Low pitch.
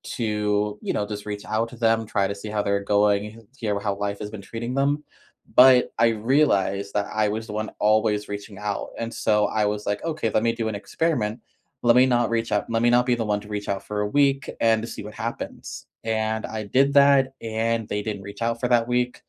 Yes: low, 110 Hz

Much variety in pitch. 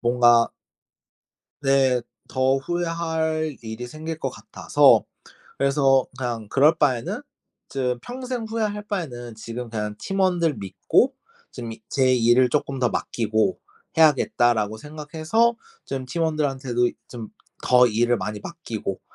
No: average, 5.0 semitones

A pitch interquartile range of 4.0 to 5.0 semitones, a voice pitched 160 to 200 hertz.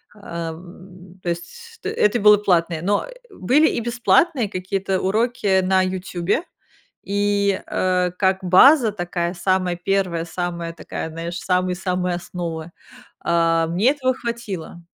No: average, 3.0 semitones; medium, 185 Hz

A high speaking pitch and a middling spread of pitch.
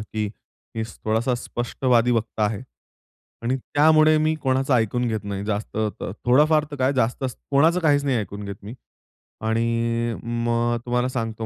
No: low, 120 Hz; average, 3.1 semitones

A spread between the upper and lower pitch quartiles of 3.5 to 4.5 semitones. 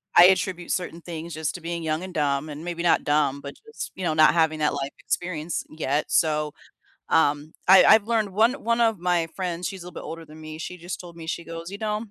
No: average, 2.7 semitones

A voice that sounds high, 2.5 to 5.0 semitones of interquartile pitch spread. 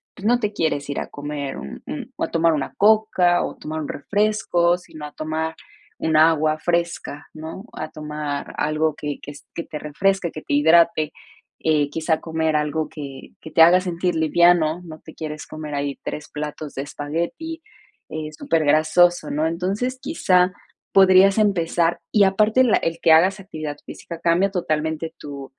No: medium, 160 Hz; average, 2.9 semitones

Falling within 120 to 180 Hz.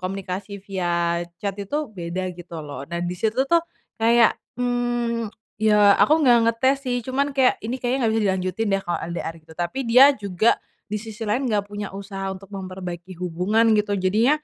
No: high, 210 Hz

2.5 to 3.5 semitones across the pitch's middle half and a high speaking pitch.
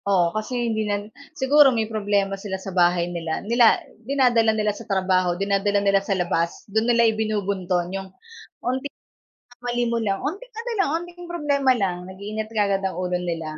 No: average, 4.1 semitones; high, 205 Hz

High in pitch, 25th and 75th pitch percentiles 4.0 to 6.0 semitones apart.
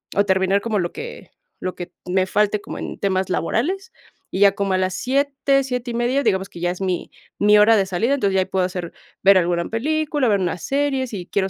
Yes: high, 200 Hz; average, 5.1 semitones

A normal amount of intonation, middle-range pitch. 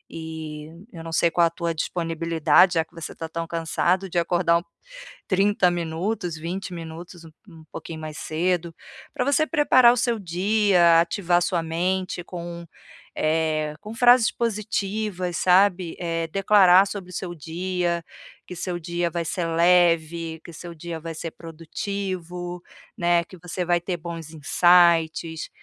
No: narrow, 2.0 semitones; medium, 175 Hz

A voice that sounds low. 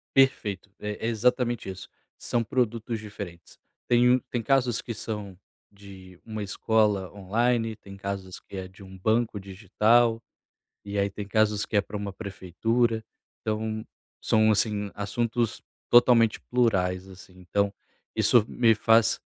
Yes: low, 105 Hz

